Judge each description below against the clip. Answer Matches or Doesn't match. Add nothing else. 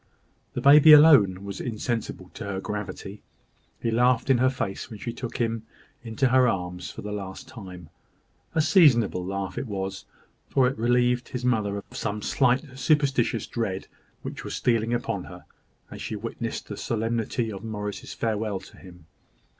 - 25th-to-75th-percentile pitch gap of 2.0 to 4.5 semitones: Matches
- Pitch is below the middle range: Matches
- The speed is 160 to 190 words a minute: Matches